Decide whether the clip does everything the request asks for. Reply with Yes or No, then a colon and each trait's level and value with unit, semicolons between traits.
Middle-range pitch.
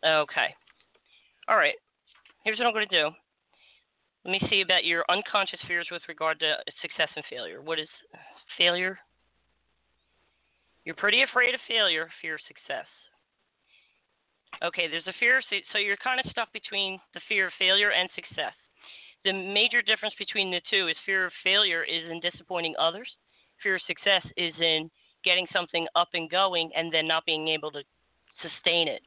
Yes: medium, 180 Hz